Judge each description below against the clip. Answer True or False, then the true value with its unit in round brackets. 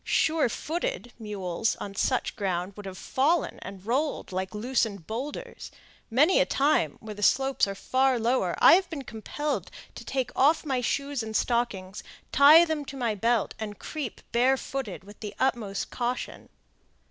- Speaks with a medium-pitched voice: False (240 Hz)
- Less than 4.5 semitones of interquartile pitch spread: False (5.1 semitones)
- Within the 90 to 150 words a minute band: False (160 wpm)